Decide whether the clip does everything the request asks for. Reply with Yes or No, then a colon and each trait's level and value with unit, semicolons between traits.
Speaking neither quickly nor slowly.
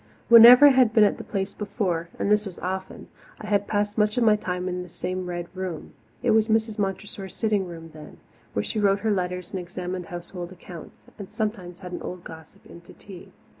No: fast, 215 wpm